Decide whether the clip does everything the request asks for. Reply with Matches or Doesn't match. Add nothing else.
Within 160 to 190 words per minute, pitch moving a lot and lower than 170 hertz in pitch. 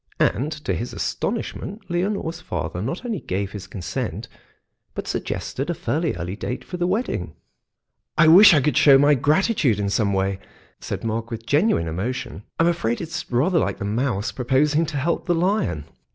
Matches